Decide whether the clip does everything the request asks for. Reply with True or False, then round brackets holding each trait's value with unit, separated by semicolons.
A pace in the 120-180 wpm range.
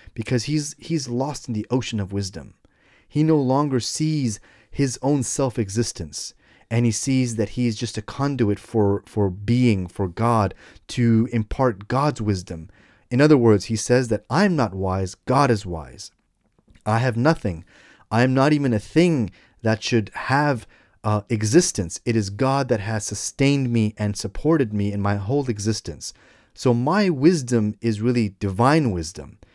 True (165 wpm)